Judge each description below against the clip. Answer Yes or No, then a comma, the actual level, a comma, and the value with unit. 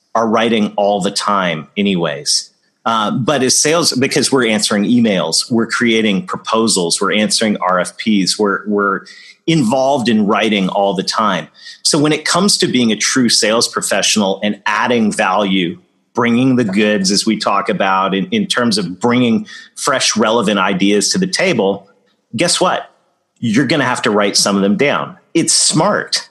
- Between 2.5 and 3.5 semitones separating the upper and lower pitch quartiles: No, average, 4.6 semitones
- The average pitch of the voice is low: Yes, low, 110 Hz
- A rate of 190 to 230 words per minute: No, average, 165 wpm